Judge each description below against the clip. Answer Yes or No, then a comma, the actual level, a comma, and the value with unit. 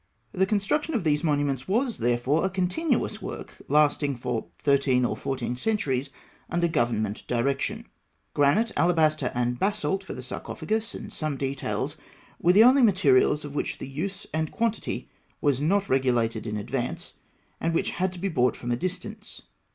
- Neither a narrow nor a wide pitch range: No, wide, 7.1 semitones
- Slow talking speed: No, average, 165 wpm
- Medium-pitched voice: Yes, medium, 150 Hz